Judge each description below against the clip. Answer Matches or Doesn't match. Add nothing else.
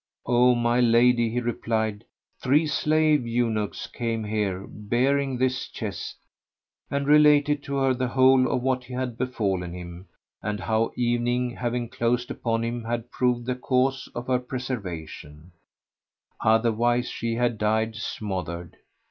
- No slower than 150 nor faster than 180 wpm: Doesn't match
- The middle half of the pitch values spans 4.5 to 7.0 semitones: Doesn't match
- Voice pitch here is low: Matches